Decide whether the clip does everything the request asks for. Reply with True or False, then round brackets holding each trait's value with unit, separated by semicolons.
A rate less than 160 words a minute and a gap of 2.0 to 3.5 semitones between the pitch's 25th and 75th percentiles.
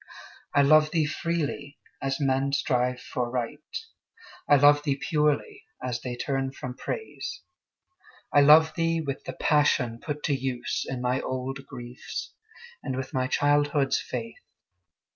True (145 wpm; 2.7 semitones)